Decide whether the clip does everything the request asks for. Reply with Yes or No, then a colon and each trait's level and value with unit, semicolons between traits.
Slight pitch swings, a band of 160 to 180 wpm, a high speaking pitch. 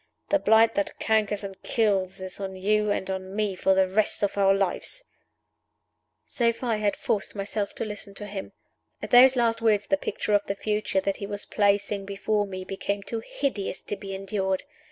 No: narrow, 1.7 semitones; average, 195 wpm; high, 205 Hz